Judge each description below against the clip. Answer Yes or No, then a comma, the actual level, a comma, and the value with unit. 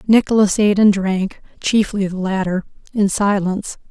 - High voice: Yes, high, 200 Hz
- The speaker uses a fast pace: No, average, 140 wpm